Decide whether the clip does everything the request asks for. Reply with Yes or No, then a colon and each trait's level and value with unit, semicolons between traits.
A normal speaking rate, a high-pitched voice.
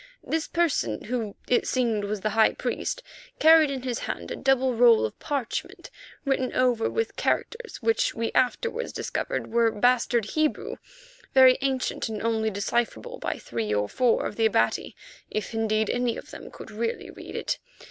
Yes: average, 170 wpm; high, 235 Hz